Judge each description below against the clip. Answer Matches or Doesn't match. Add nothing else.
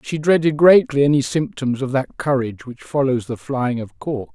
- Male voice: Matches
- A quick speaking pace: Doesn't match